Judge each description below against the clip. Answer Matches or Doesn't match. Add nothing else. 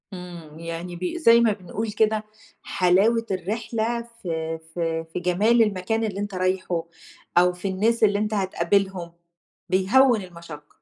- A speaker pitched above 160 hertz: Matches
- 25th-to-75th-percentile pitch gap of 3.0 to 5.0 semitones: Matches